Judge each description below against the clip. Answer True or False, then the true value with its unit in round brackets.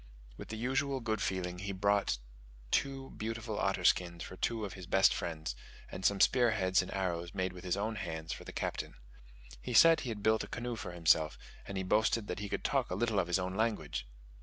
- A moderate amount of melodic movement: True (3.8 semitones)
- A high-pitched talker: False (100 Hz)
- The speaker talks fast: True (220 wpm)